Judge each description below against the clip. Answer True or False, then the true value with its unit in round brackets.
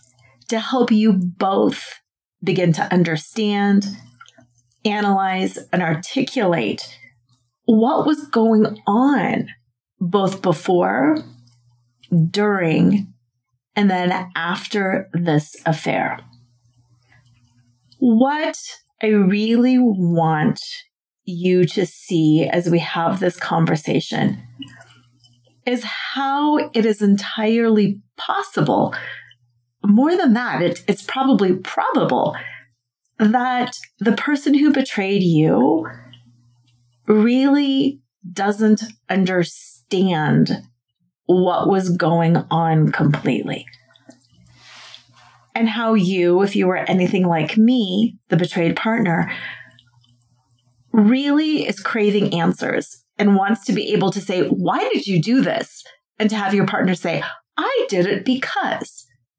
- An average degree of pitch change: False (8.2 semitones)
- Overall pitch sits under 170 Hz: False (185 Hz)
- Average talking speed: False (100 wpm)